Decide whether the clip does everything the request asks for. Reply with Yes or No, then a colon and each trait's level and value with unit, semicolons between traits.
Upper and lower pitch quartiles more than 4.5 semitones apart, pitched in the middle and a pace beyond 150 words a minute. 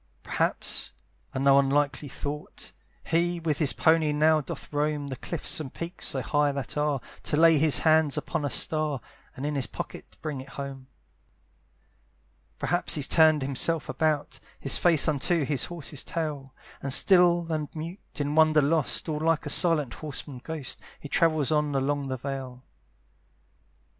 No: narrow, 2.4 semitones; medium, 150 Hz; average, 160 wpm